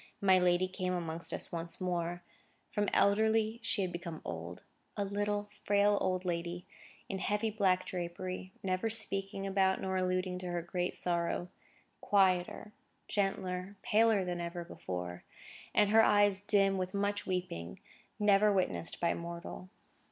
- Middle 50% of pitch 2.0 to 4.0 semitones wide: Yes, narrow, 2.6 semitones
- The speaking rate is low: No, average, 145 wpm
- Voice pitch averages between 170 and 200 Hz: Yes, medium, 185 Hz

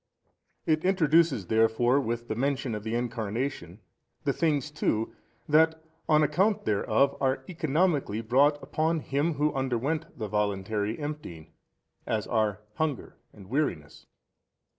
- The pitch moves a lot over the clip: Yes, wide, 5.7 semitones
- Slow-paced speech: Yes, slow, 130 wpm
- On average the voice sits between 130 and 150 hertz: Yes, low, 135 Hz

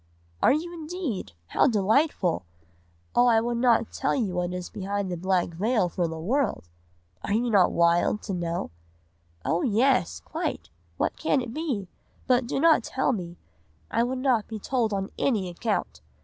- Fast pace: No, average, 170 wpm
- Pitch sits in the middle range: No, high, 220 Hz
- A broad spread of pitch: Yes, wide, 5.9 semitones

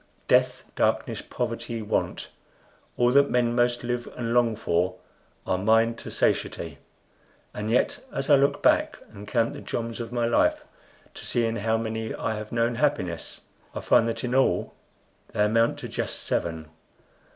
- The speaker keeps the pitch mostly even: Yes, narrow, 1.6 semitones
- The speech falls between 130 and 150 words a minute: No, average, 165 wpm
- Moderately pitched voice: No, low, 115 Hz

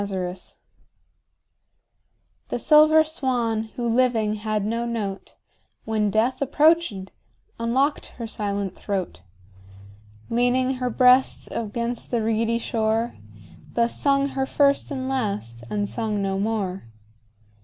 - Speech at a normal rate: No, slow, 115 wpm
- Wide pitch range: No, average, 3.7 semitones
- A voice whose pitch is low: No, high, 230 Hz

